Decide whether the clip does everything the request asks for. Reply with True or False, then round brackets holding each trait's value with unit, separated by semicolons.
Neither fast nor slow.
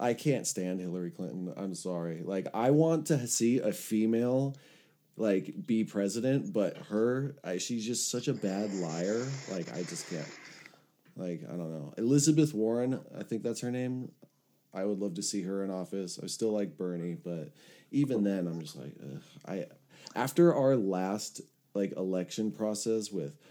True (175 wpm)